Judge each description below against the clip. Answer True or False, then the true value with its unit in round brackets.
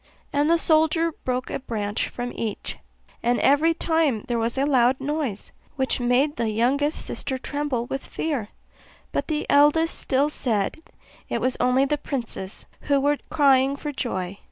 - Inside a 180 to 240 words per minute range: False (160 wpm)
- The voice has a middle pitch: False (270 Hz)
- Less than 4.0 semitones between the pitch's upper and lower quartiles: True (3.5 semitones)